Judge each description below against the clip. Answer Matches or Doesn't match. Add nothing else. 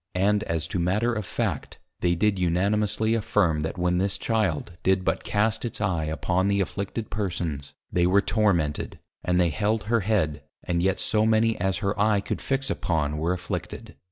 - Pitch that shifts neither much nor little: Matches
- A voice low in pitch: Matches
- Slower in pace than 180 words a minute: Doesn't match